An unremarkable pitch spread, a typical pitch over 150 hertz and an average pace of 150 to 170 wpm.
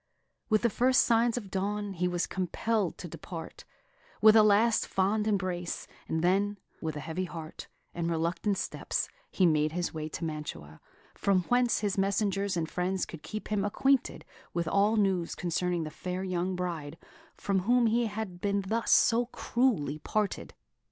Yes: average, 3.8 semitones; high, 190 Hz; average, 165 wpm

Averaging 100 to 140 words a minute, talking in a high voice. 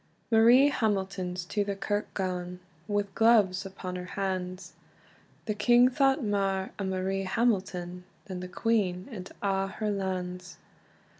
Yes: slow, 135 wpm; high, 195 Hz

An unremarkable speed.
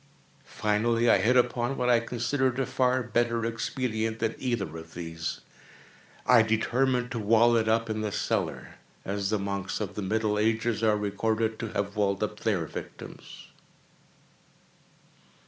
Yes: average, 145 wpm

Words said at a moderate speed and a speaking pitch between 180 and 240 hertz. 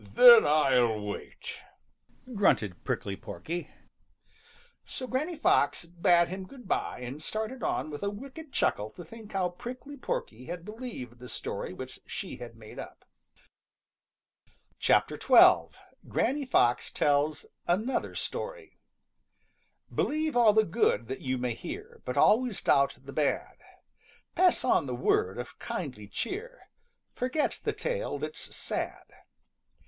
No: slow, 130 wpm; medium, 185 Hz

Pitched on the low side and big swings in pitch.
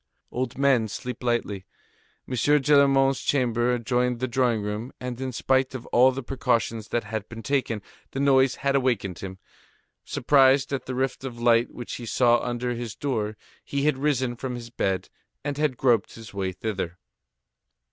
No: low, 125 Hz; narrow, 2.6 semitones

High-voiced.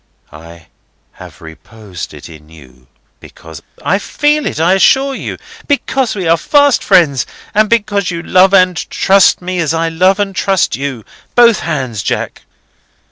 No: medium, 180 Hz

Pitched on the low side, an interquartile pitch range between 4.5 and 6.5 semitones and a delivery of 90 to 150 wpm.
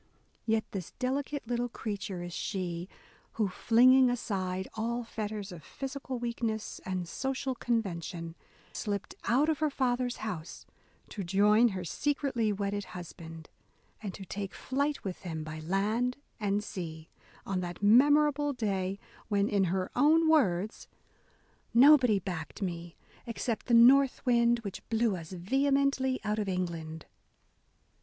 No: high, 210 Hz; average, 5.2 semitones; average, 140 wpm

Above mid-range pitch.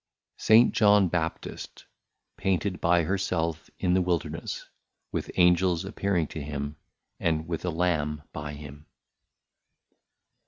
No: very low, 85 Hz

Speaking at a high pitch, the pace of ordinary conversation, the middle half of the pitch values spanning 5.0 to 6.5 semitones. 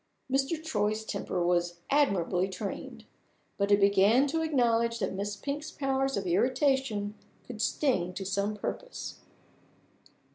No: high, 225 Hz; slow, 130 wpm; wide, 5.4 semitones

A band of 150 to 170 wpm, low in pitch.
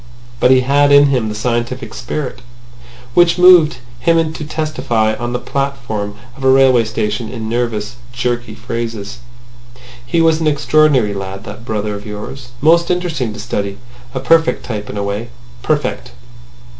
Yes: average, 155 wpm; low, 120 Hz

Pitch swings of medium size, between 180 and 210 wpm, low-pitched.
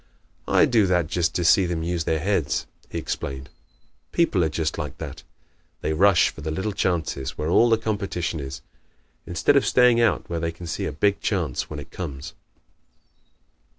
Yes: average, 4.2 semitones; average, 185 wpm; very low, 85 Hz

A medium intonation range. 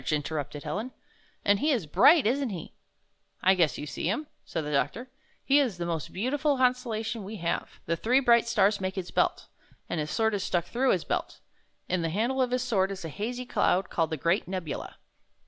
No: wide, 6.7 semitones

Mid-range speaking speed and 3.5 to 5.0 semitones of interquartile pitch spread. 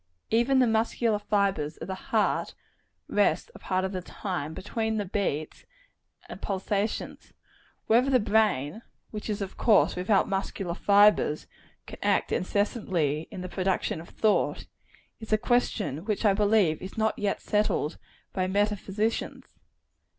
No: average, 145 wpm; average, 2.9 semitones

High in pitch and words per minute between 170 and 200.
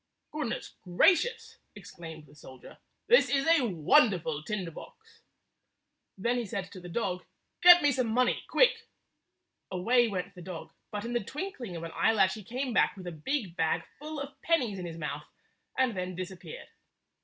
Yes: high, 205 Hz; average, 180 wpm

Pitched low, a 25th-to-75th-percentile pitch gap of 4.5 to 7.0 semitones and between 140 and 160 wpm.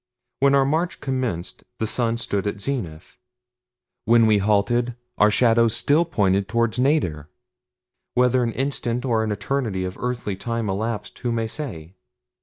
No: low, 115 Hz; average, 3.6 semitones; average, 150 wpm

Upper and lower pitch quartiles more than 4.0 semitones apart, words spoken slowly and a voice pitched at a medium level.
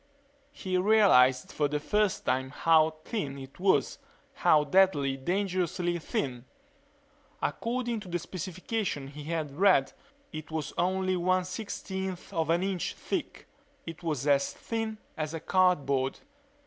Yes: average, 4.6 semitones; slow, 130 wpm; medium, 170 Hz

